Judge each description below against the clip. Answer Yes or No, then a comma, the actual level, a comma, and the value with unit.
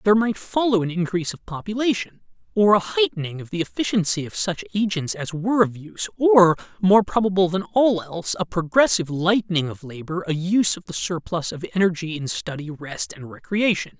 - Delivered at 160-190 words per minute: Yes, average, 180 wpm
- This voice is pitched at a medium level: Yes, medium, 180 Hz